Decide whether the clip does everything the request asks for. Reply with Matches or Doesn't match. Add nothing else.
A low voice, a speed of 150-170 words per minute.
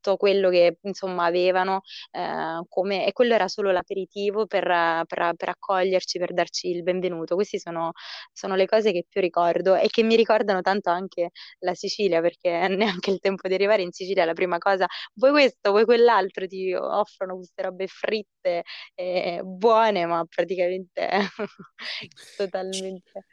Doesn't match